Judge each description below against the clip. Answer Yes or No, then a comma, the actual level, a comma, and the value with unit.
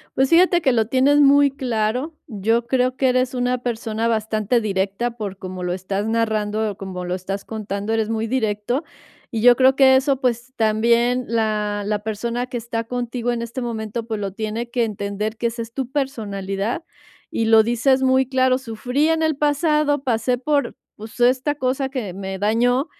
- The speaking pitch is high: Yes, high, 235 Hz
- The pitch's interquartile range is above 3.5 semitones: No, average, 3.2 semitones